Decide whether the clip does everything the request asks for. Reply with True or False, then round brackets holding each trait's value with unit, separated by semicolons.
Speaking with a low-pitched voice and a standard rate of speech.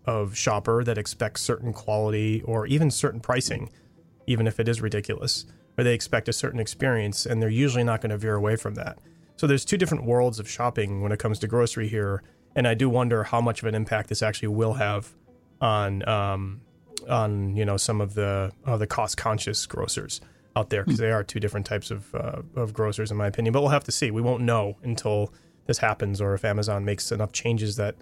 False (110 Hz; 220 wpm)